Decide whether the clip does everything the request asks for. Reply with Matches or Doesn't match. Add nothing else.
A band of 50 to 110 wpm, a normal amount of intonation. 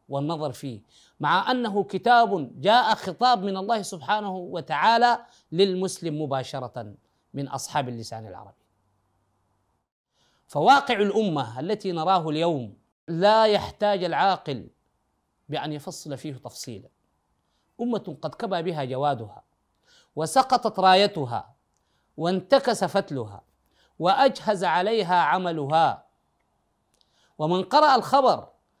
Doesn't match